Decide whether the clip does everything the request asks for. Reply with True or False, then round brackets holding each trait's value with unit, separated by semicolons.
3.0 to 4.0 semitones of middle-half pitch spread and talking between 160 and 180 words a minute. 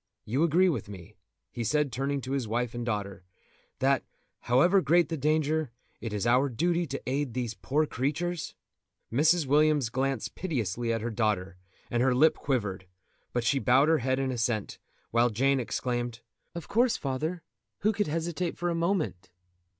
False (4.9 semitones; 170 wpm)